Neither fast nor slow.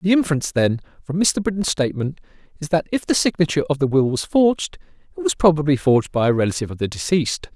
No: fast, 215 wpm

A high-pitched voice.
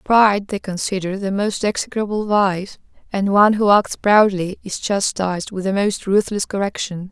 Yes: high, 200 Hz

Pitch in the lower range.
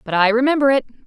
No: high, 245 Hz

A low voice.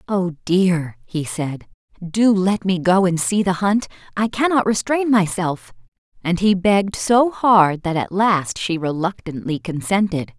No: medium, 185 Hz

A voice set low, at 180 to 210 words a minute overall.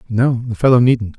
Yes: low, 120 Hz; fast, 205 wpm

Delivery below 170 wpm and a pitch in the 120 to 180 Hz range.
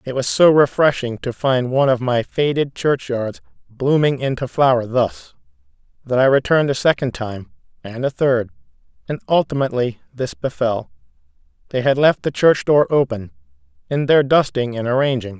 Yes: average, 155 wpm; low, 130 Hz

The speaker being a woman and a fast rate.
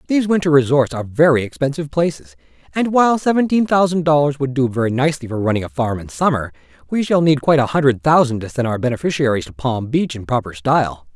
No: male; fast, 210 wpm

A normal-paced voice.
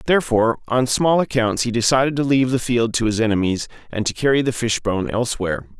Yes: average, 195 wpm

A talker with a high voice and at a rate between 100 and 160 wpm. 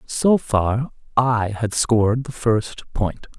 No: low, 115 Hz; average, 140 wpm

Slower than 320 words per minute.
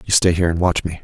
No: fast, 350 wpm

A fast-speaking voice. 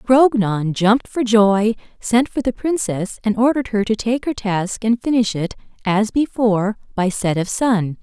No: average, 180 wpm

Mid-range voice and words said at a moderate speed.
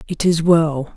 Yes: medium, 160 Hz; average, 190 wpm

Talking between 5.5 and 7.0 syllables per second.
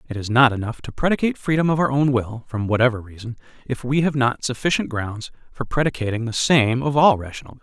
Yes: 6.2 syllables/s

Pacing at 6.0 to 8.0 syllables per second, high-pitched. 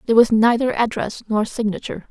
Yes: 6.3 syllables/s; high, 225 Hz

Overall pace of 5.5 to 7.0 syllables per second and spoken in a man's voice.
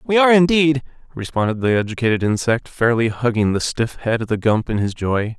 Yes: 5.7 syllables/s; male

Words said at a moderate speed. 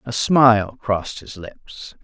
Yes: average, 145 wpm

